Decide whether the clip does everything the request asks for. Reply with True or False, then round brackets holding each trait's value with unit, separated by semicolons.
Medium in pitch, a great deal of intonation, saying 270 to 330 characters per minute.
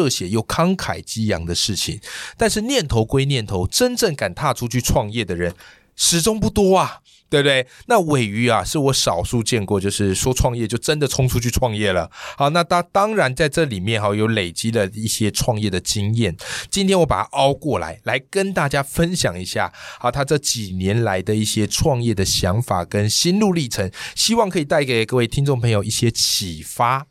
False (120 Hz; 6.3 semitones; 290 characters per minute)